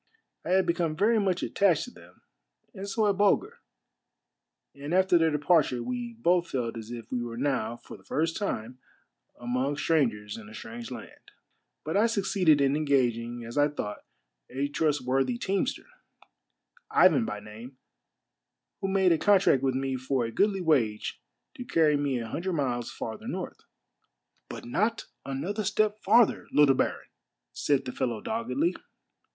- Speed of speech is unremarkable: Yes, average, 165 wpm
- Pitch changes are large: Yes, wide, 7.8 semitones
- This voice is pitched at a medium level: Yes, medium, 145 Hz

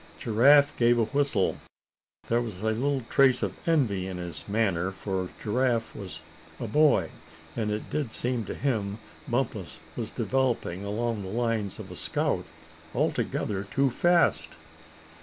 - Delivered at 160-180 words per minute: No, average, 145 wpm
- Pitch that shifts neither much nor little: Yes, average, 4.4 semitones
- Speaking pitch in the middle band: No, low, 115 Hz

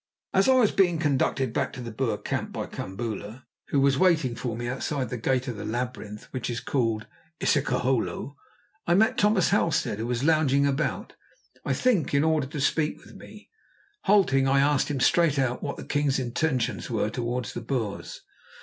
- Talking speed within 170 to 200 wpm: Yes, average, 185 wpm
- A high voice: No, low, 135 Hz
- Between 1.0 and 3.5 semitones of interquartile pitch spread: No, average, 4.4 semitones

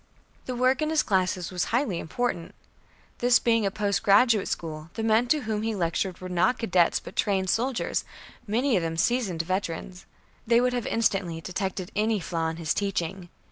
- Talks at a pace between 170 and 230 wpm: Yes, average, 180 wpm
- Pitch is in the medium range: No, high, 200 Hz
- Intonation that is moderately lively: Yes, average, 4.9 semitones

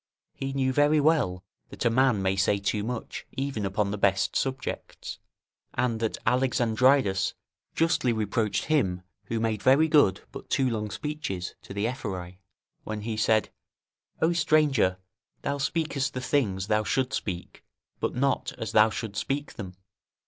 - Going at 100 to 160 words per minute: Yes, average, 155 wpm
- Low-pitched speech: Yes, low, 115 Hz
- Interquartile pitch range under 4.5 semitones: No, average, 5.2 semitones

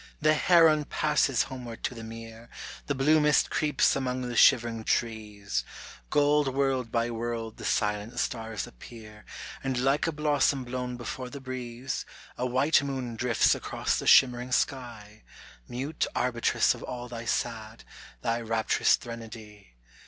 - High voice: No, low, 125 Hz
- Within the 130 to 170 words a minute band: Yes, average, 145 wpm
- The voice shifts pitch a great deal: No, average, 2.9 semitones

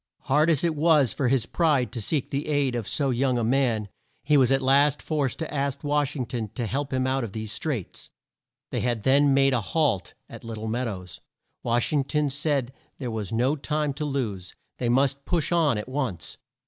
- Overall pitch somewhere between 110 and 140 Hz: Yes, low, 135 Hz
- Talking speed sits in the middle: No, fast, 215 wpm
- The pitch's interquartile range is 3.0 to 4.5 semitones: Yes, average, 3.5 semitones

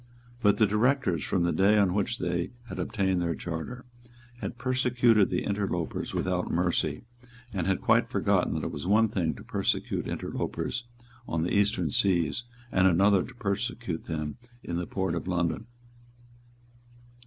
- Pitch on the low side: Yes, very low, 95 Hz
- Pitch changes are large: No, average, 3.6 semitones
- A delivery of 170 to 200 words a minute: No, average, 155 wpm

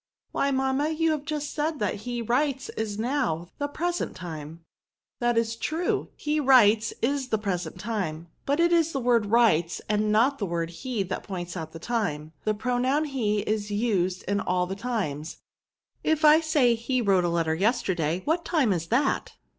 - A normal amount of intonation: No, wide, 7.1 semitones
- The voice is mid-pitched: No, high, 230 Hz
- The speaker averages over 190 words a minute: Yes, average, 200 wpm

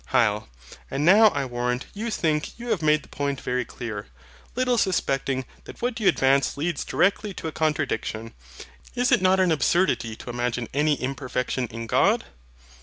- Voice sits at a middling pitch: Yes, medium, 145 Hz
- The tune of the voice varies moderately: No, wide, 7.0 semitones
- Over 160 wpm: Yes, average, 170 wpm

